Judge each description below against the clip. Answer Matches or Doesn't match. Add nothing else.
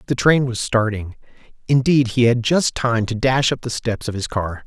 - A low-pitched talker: Matches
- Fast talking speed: Matches